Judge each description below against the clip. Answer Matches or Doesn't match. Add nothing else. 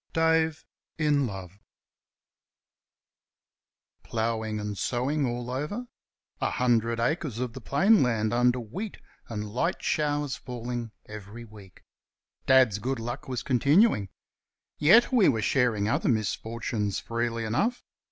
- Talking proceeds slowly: Matches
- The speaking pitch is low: Matches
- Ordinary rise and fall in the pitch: Matches